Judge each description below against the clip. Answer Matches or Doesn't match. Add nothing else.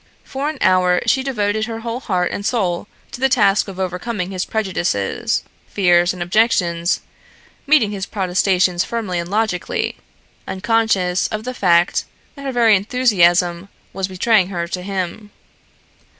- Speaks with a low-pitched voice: Doesn't match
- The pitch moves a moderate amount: Matches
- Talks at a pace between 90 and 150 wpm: Matches